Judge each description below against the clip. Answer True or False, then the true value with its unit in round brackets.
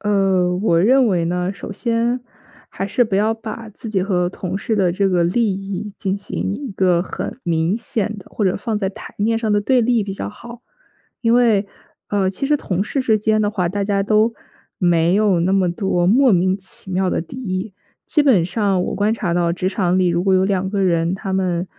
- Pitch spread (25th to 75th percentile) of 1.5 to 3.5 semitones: True (3.1 semitones)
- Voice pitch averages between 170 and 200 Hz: True (195 Hz)